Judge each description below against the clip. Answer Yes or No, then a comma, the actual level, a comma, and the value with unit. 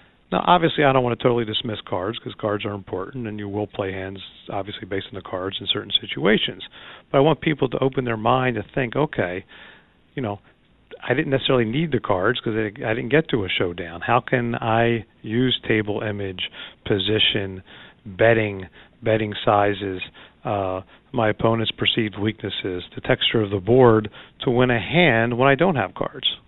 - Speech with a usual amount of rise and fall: Yes, average, 3.7 semitones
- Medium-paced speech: Yes, average, 185 wpm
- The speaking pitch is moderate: No, low, 110 Hz